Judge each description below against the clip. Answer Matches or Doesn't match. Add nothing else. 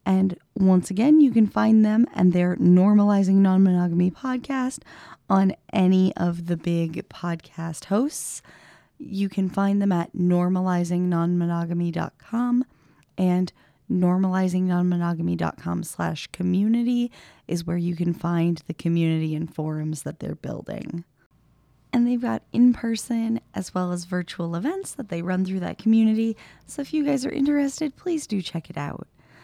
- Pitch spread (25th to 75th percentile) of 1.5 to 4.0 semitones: Doesn't match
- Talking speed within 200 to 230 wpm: Doesn't match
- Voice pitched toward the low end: Doesn't match